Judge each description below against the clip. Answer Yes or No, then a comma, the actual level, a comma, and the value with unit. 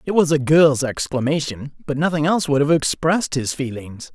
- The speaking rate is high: No, average, 190 wpm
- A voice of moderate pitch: Yes, medium, 145 Hz